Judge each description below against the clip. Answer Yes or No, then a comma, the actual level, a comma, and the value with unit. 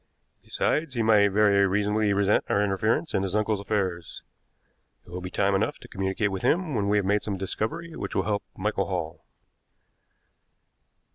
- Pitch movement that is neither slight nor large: No, narrow, 1.9 semitones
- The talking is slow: No, average, 170 wpm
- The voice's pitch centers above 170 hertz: No, low, 100 Hz